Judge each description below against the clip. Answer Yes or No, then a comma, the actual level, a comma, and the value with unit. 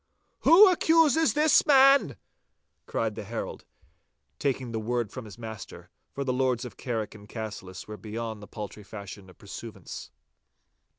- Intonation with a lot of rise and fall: No, average, 4.6 semitones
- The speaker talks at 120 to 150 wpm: Yes, average, 145 wpm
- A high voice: No, low, 115 Hz